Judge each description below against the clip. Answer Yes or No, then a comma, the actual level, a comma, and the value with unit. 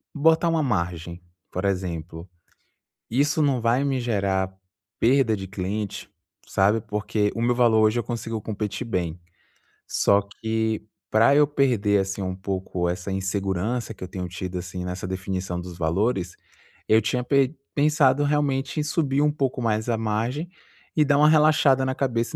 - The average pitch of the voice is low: Yes, low, 110 Hz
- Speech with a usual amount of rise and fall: No, wide, 6.0 semitones